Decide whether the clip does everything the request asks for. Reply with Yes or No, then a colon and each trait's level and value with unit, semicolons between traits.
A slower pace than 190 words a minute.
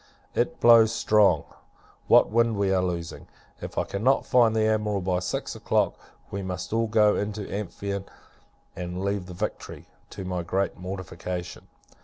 Yes: average, 160 wpm